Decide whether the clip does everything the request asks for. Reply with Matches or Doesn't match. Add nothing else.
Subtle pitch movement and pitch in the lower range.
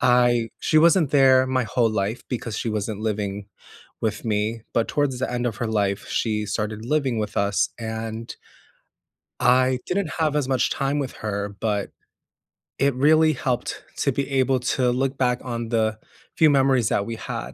Doesn't match